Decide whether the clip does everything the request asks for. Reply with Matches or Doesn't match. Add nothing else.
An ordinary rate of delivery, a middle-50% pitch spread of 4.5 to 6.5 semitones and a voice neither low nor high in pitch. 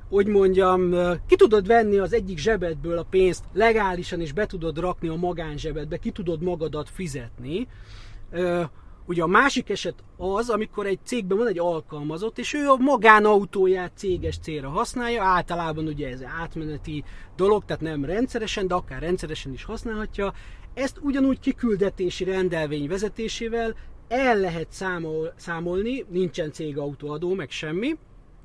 Matches